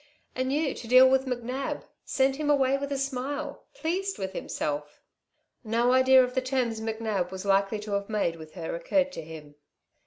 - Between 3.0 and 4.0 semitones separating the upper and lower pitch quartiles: No, wide, 5.4 semitones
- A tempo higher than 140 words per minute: Yes, average, 185 wpm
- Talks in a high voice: Yes, very high, 250 Hz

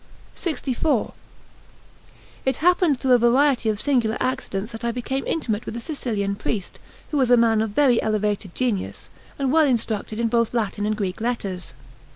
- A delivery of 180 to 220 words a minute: No, average, 170 wpm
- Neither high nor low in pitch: No, high, 235 Hz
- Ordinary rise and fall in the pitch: Yes, average, 3.8 semitones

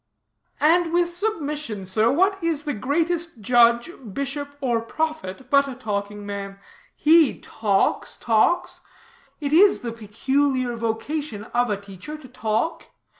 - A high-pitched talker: Yes, very high, 260 Hz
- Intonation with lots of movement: Yes, wide, 6.0 semitones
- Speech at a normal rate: No, slow, 130 wpm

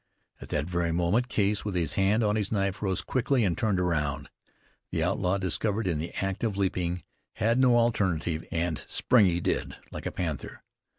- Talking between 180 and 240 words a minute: Yes, average, 185 wpm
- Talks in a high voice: No, very low, 95 Hz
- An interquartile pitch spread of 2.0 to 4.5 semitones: Yes, average, 3.9 semitones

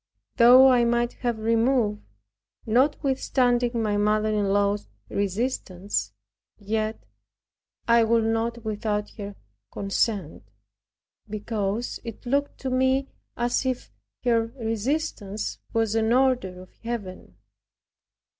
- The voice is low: No, high, 225 Hz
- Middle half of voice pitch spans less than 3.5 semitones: Yes, average, 2.9 semitones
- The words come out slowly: Yes, slow, 105 wpm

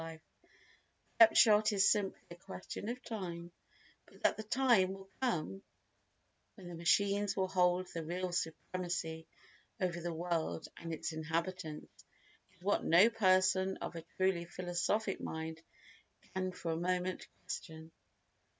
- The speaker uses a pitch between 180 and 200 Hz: Yes, medium, 185 Hz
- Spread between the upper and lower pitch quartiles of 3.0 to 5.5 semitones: No, narrow, 2.5 semitones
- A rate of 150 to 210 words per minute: No, slow, 135 wpm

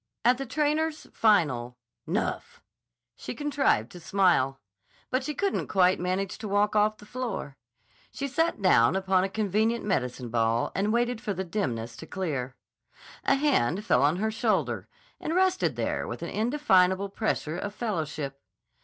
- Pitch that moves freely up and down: Yes, wide, 6.9 semitones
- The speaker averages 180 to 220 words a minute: No, average, 155 wpm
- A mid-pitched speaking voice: No, high, 200 Hz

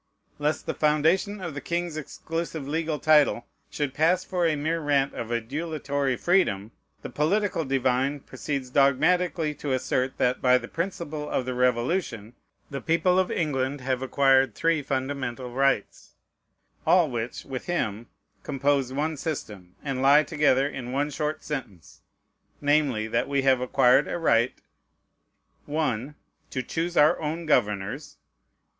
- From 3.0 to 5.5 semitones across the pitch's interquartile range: Yes, average, 3.6 semitones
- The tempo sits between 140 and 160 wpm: Yes, average, 145 wpm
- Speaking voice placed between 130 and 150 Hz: Yes, medium, 140 Hz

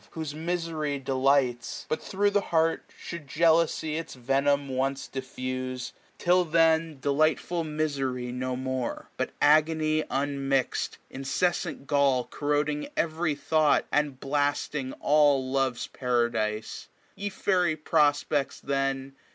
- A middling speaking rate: No, slow, 115 wpm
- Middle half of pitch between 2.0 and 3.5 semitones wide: Yes, average, 2.9 semitones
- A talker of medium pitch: Yes, medium, 145 Hz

